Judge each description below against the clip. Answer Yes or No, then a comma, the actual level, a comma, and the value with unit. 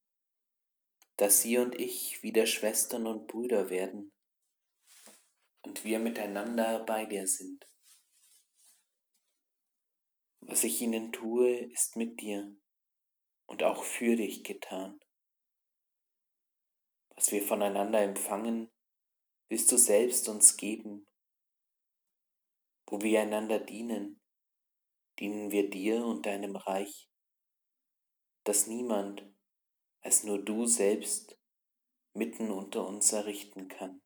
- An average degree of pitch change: No, narrow, 2.0 semitones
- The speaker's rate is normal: No, slow, 100 wpm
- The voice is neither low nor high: No, low, 105 Hz